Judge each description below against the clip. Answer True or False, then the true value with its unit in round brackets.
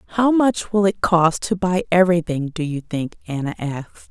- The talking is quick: False (190 wpm)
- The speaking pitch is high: False (175 Hz)